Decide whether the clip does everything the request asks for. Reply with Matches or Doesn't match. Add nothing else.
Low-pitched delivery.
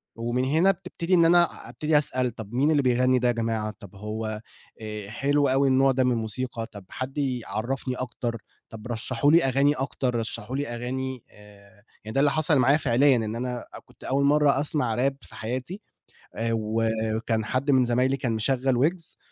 Matches